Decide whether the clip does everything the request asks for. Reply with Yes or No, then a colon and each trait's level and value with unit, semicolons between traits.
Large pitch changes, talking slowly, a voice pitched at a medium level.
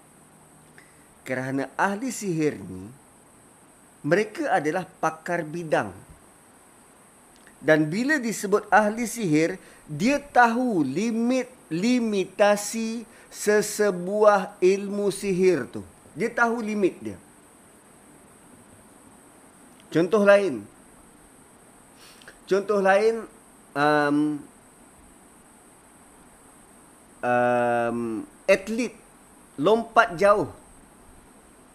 No: wide, 6.6 semitones; slow, 60 wpm; high, 195 Hz